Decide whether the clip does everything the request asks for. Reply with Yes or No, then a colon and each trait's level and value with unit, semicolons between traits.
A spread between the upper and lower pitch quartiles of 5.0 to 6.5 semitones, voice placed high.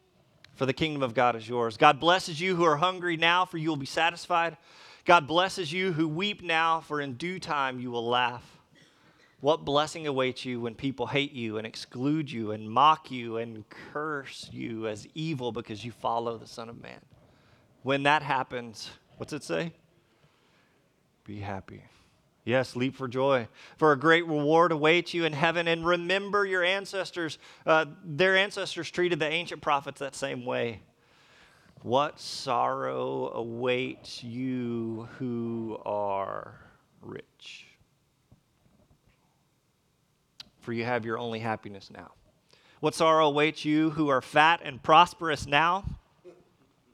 No: wide, 5.6 semitones; medium, 145 Hz